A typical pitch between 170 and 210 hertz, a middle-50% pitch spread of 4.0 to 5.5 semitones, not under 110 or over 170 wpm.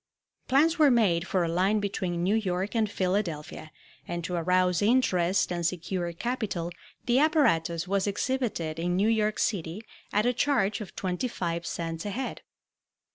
Yes: high, 190 Hz; average, 4.4 semitones; average, 160 wpm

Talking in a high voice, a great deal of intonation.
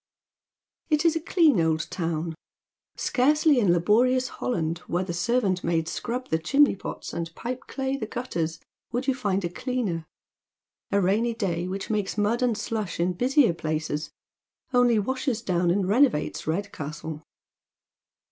Yes: high, 205 Hz; wide, 6.8 semitones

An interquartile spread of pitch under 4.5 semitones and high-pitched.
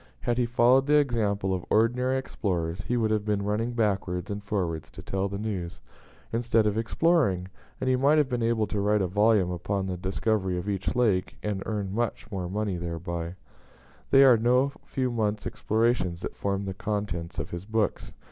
No: average, 3.8 semitones; low, 105 Hz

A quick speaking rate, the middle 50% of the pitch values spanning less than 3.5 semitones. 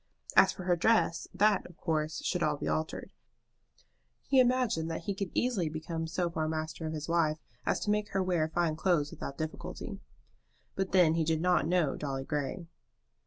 No: average, 185 wpm; average, 2.9 semitones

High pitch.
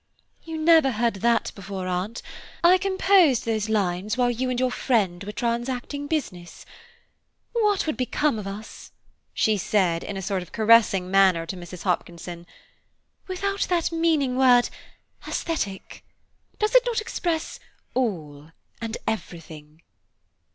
Yes: high, 230 Hz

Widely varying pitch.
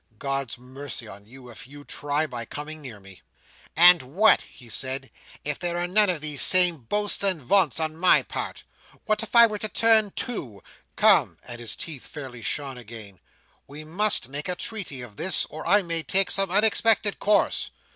Yes: wide, 7.2 semitones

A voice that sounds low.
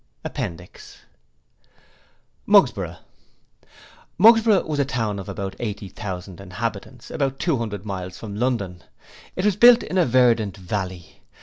Yes: low, 110 Hz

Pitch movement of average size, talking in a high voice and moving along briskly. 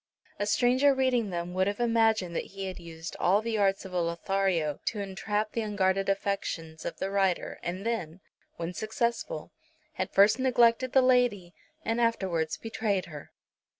No: average, 4.3 semitones; high, 200 Hz; average, 165 wpm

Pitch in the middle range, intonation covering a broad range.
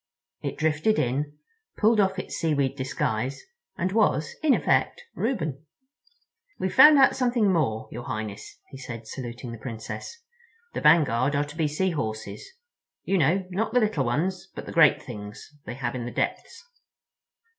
Yes: medium, 145 Hz; wide, 7.7 semitones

